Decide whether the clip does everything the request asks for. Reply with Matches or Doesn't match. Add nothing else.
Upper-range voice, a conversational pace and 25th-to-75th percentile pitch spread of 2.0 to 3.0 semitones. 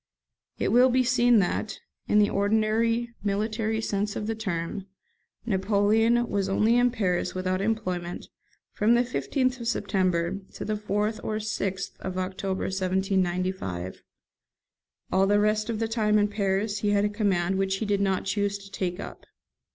Matches